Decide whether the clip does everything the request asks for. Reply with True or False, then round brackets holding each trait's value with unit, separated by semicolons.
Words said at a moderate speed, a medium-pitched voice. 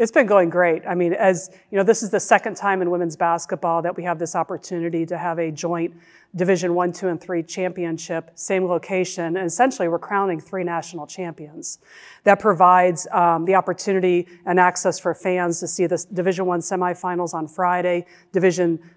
True (190 wpm; 180 Hz)